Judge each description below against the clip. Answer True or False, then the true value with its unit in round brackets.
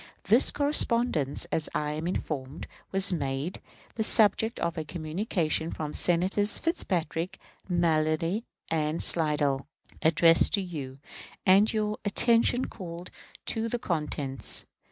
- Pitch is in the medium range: True (170 Hz)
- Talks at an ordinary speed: False (115 wpm)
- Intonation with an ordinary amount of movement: True (5.0 semitones)